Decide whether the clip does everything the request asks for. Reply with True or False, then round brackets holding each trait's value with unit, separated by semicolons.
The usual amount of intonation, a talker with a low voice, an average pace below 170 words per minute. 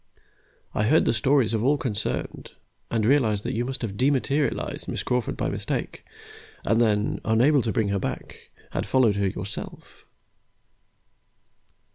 True (3.9 semitones; 115 Hz; 145 wpm)